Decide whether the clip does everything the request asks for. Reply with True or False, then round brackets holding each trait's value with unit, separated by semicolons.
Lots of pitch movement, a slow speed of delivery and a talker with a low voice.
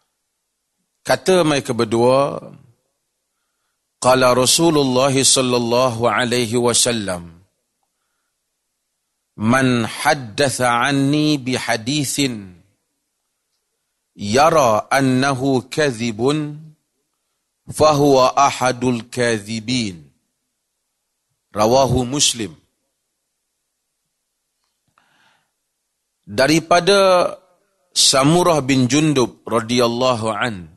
False (2.9 semitones; 55 wpm; 125 Hz)